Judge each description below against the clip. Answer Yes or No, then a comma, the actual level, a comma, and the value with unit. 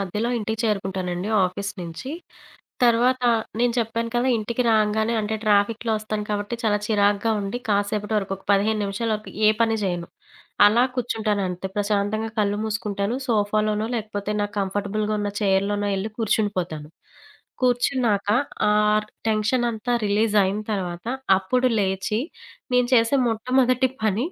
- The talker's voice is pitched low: No, high, 210 Hz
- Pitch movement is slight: Yes, narrow, 2.1 semitones